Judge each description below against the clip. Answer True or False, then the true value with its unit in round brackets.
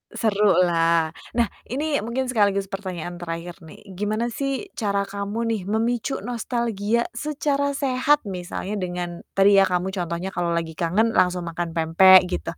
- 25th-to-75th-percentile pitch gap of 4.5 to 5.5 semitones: True (5.0 semitones)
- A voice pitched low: False (200 Hz)